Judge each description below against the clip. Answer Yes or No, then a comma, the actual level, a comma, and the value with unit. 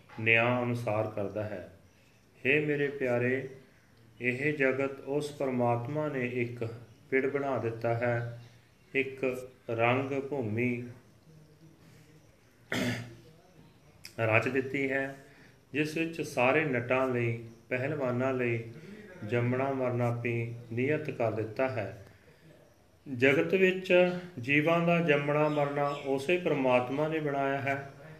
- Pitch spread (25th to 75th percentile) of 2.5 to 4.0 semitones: Yes, average, 3.4 semitones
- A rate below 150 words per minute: Yes, average, 100 wpm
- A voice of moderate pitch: No, low, 130 Hz